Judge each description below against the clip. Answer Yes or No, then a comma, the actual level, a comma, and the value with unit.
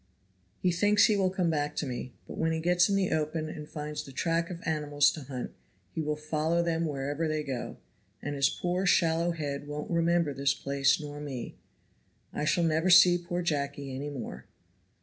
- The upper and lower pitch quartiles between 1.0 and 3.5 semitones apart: Yes, average, 2.8 semitones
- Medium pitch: Yes, medium, 155 Hz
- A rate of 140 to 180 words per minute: No, average, 195 wpm